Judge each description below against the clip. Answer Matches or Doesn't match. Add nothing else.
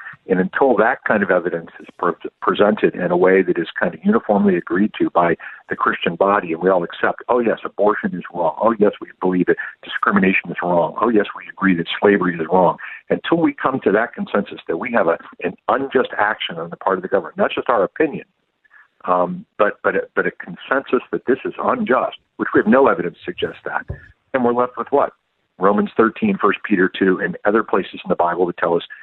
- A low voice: Matches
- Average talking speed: Doesn't match